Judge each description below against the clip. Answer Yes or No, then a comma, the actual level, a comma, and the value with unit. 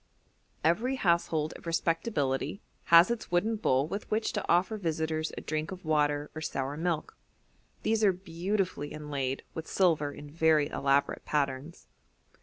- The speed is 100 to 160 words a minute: Yes, average, 145 wpm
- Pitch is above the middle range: No, medium, 160 Hz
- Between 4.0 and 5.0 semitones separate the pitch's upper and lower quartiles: No, average, 3.6 semitones